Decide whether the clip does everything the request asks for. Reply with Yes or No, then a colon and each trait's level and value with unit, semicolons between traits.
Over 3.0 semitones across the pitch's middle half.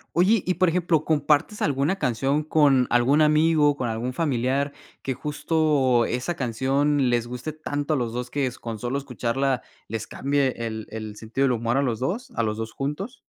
Yes: average, 3.9 semitones